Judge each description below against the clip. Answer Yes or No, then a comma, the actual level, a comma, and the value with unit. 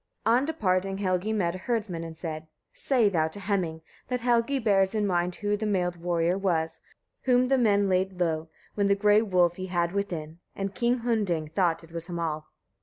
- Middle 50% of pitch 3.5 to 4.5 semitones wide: Yes, average, 3.8 semitones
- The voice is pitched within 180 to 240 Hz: Yes, high, 190 Hz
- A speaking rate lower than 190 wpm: No, average, 195 wpm